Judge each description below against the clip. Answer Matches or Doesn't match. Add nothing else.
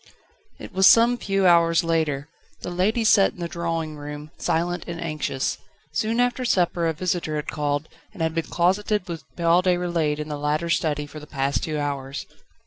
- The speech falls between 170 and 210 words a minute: Matches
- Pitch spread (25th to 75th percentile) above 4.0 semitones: Doesn't match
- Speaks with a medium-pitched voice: Matches